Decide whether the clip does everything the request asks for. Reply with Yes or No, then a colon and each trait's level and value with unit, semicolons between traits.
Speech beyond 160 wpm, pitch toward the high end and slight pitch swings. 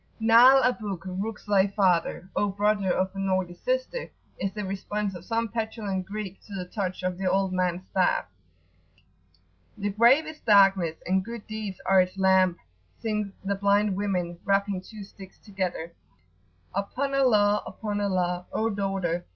No: average, 155 wpm; high, 195 Hz; narrow, 2.3 semitones